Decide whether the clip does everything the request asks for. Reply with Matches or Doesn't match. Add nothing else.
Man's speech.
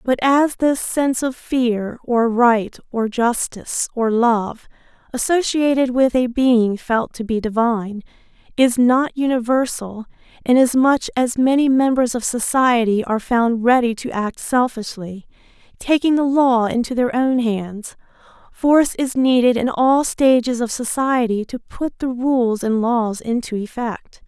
Doesn't match